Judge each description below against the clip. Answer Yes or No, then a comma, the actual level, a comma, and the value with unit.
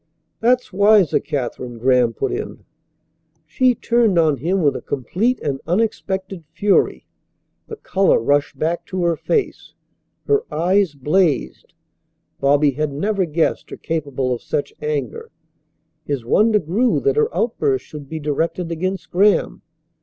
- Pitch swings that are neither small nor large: No, wide, 6.1 semitones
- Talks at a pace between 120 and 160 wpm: Yes, average, 140 wpm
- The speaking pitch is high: No, medium, 170 Hz